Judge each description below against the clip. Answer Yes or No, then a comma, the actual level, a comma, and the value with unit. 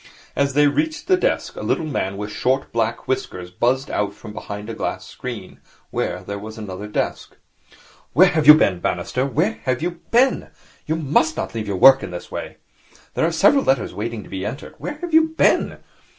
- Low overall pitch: Yes, low, 130 Hz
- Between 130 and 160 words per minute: No, average, 200 wpm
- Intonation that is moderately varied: No, wide, 7.5 semitones